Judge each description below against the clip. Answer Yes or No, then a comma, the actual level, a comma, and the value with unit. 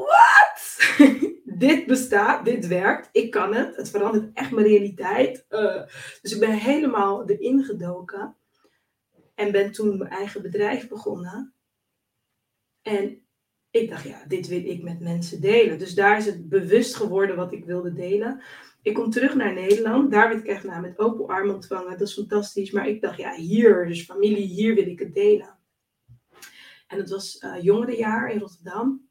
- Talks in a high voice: Yes, high, 205 Hz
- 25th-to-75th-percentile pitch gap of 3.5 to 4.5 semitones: No, average, 3.1 semitones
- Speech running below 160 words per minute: No, average, 170 wpm